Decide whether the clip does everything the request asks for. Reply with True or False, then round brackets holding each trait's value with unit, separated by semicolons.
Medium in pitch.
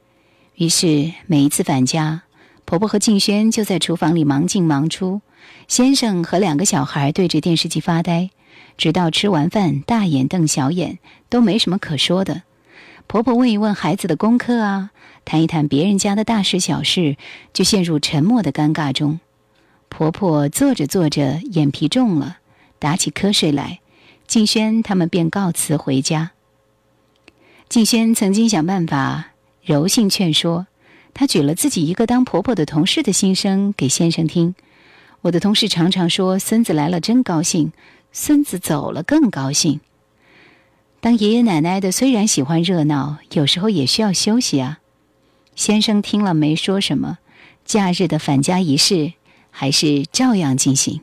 True (170 Hz)